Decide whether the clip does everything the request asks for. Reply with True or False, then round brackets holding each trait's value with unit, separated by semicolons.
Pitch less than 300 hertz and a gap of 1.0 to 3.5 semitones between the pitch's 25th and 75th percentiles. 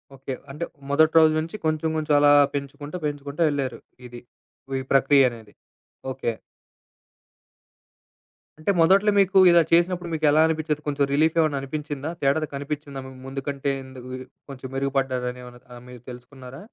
True (140 Hz; 2.9 semitones)